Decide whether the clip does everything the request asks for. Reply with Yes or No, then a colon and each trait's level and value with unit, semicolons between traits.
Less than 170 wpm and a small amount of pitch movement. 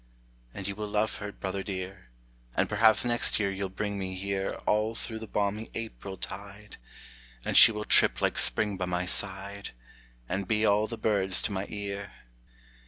No: average, 175 wpm; narrow, 1.7 semitones